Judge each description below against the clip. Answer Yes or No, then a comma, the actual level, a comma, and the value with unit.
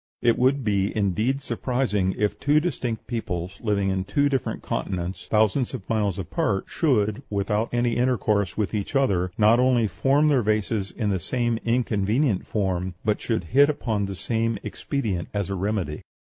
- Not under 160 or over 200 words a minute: Yes, average, 165 wpm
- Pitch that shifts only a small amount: No, average, 4.2 semitones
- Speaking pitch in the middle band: No, low, 110 Hz